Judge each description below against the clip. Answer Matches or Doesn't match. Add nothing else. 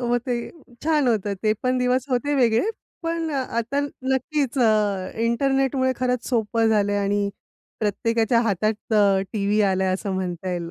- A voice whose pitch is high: Matches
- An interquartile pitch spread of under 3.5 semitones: Doesn't match